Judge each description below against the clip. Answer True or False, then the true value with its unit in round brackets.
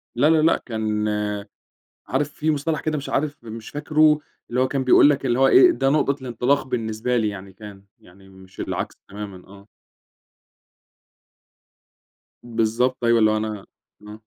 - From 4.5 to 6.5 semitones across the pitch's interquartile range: True (5.0 semitones)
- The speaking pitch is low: True (120 Hz)